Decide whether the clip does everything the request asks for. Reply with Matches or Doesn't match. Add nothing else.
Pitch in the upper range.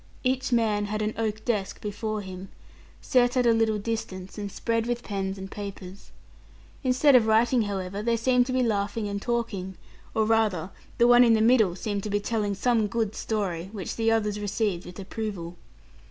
Matches